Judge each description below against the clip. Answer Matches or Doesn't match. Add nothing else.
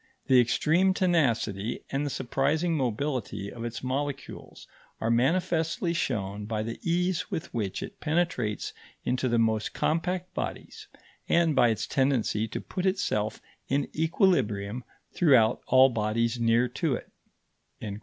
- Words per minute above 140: Doesn't match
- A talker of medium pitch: Doesn't match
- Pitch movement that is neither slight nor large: Doesn't match